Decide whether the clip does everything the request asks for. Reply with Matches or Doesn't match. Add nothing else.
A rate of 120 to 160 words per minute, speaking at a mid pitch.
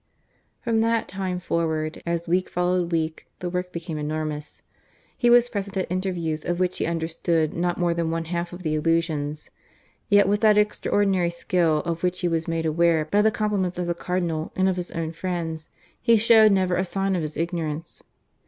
Doesn't match